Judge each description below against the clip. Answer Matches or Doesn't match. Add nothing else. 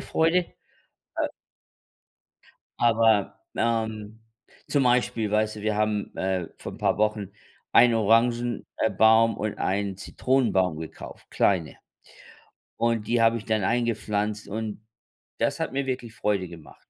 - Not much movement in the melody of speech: Matches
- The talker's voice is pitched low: Matches